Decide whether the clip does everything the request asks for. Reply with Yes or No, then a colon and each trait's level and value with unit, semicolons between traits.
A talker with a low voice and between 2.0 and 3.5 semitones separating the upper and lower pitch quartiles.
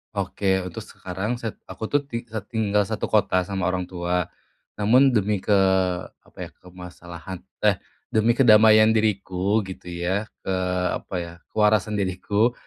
Yes: low, 100 Hz; average, 3.0 semitones